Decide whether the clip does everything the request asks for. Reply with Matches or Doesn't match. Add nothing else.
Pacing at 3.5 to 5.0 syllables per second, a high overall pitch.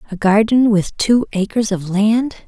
Matches